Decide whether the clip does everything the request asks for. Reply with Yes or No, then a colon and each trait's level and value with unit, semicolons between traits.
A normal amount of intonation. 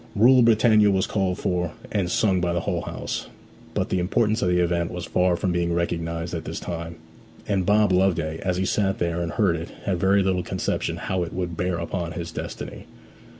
No: narrow, 2.2 semitones